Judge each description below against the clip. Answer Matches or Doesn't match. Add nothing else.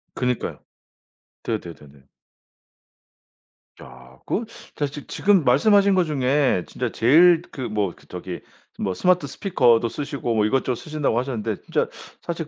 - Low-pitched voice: Matches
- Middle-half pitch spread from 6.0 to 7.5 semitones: Matches